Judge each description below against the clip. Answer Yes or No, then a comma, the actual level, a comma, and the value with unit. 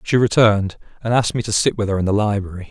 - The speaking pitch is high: No, low, 105 Hz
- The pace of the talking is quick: Yes, fast, 265 wpm